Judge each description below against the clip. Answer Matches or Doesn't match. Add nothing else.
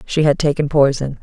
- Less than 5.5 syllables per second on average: Matches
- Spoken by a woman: Matches